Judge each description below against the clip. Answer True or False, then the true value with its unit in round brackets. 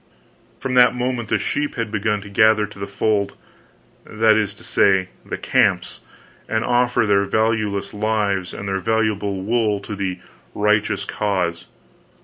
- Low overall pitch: True (105 Hz)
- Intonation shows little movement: True (2.1 semitones)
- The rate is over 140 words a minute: True (150 wpm)